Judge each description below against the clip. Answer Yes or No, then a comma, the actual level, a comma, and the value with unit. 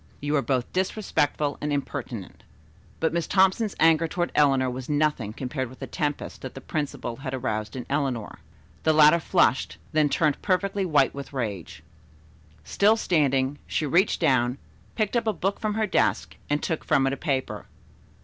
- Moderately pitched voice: Yes, medium, 145 Hz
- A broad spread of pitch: No, average, 4.5 semitones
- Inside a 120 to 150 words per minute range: No, average, 170 wpm